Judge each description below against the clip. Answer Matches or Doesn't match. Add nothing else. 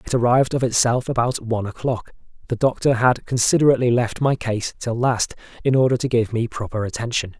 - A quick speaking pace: Doesn't match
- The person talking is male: Matches